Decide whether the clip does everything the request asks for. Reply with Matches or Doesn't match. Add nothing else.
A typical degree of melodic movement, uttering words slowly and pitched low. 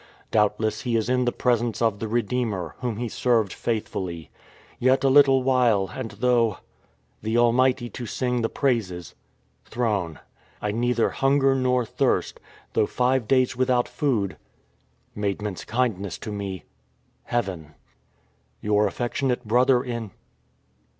Matches